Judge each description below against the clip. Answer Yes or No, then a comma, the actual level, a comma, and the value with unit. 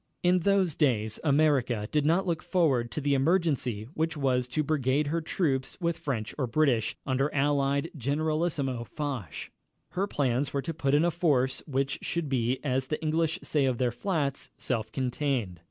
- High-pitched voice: No, medium, 140 Hz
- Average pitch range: Yes, average, 3.6 semitones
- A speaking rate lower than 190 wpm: Yes, average, 170 wpm